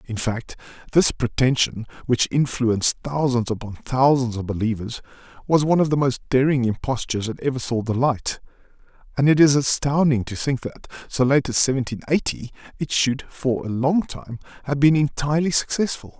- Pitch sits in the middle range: No, low, 130 Hz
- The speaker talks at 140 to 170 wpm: Yes, average, 165 wpm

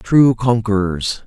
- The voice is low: Yes, low, 110 Hz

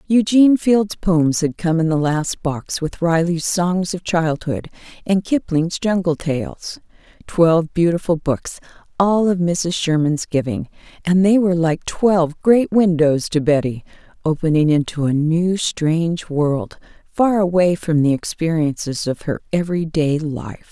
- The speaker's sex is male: No, female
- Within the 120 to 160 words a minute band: Yes, average, 150 wpm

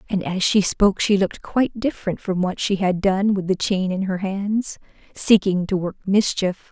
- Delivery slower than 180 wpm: No, fast, 205 wpm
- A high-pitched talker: Yes, high, 195 Hz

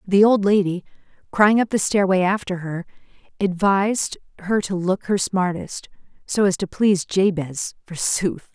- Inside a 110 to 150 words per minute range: Yes, average, 140 wpm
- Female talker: Yes, female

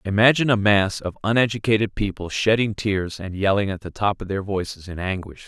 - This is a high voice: No, low, 100 Hz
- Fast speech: No, average, 195 wpm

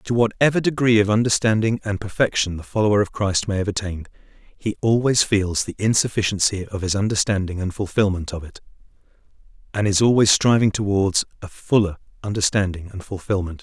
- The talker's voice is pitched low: Yes, low, 100 Hz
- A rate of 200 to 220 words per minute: No, average, 160 wpm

